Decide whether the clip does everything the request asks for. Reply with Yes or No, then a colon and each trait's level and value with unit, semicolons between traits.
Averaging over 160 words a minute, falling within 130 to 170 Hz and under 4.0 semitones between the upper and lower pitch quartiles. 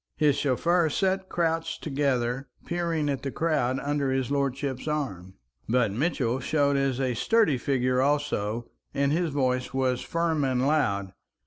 No: average, 145 wpm; medium, 140 Hz; average, 3.3 semitones